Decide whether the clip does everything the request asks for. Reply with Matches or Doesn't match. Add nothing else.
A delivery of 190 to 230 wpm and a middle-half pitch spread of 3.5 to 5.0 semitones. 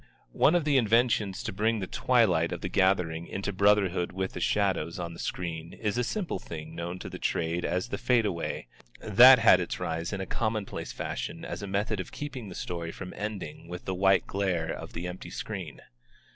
Matches